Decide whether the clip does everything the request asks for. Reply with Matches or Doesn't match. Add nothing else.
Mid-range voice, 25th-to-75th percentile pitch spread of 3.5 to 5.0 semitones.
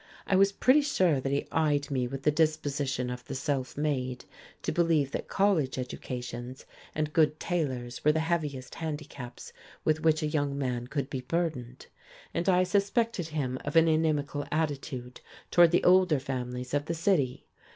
Matches